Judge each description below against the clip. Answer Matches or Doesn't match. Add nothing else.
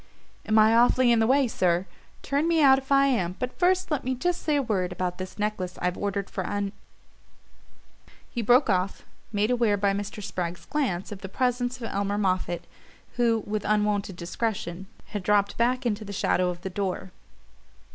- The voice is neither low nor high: Doesn't match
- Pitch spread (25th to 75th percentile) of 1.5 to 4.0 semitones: Doesn't match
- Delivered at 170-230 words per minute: Matches